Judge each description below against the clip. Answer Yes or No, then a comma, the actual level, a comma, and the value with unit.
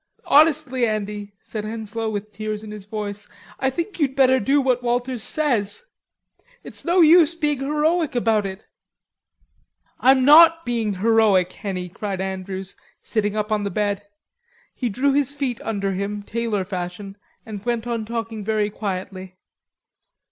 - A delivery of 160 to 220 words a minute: No, average, 150 wpm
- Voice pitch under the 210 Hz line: No, high, 220 Hz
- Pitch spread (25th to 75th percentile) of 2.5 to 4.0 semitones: No, average, 4.5 semitones